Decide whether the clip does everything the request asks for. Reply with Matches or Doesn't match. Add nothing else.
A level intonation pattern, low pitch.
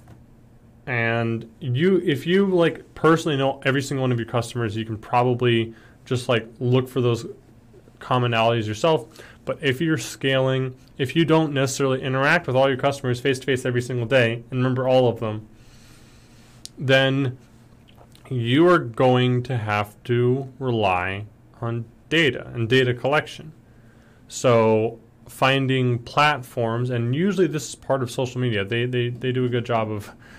Matches